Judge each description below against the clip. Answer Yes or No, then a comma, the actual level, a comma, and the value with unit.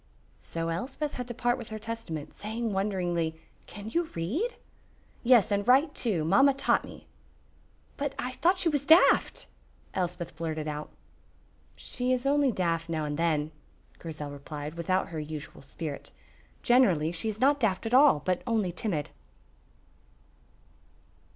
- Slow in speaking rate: No, average, 145 wpm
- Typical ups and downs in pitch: No, wide, 7.4 semitones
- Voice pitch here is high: Yes, high, 195 Hz